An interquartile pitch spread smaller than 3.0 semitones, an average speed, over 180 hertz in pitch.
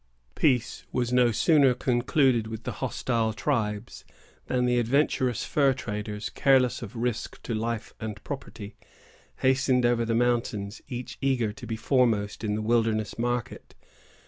No: narrow, 2.4 semitones; average, 145 wpm; low, 120 Hz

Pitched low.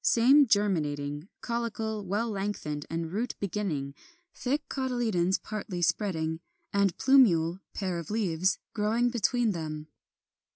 No: high, 200 Hz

